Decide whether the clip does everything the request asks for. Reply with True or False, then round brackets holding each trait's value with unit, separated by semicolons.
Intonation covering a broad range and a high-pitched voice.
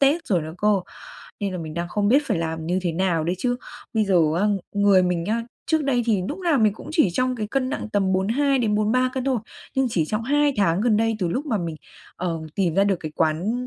True (5.9 semitones; 210 Hz)